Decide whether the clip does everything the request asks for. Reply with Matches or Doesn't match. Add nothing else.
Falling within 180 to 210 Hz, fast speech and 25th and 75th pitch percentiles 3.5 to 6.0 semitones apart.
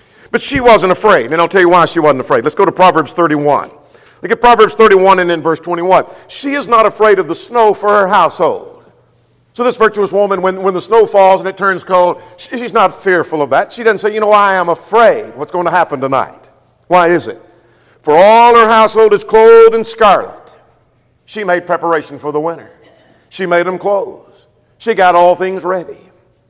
Matches